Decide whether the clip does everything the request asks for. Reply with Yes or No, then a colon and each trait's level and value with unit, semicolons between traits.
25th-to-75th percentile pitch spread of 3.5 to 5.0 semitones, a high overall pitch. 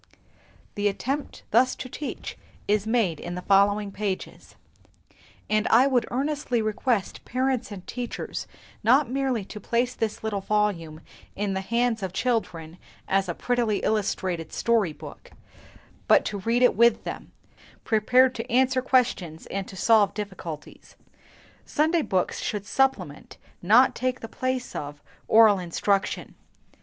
Yes: average, 4.3 semitones; high, 215 Hz